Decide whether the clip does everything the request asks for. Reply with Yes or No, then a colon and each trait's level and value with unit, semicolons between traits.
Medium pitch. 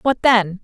No: high, 220 Hz